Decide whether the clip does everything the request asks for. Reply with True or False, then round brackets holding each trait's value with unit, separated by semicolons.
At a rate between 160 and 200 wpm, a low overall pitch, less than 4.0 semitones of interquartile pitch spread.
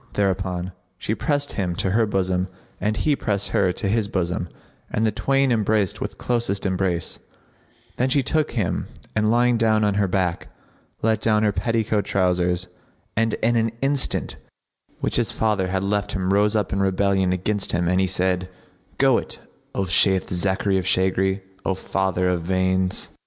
True (175 wpm; 100 Hz; 2.9 semitones)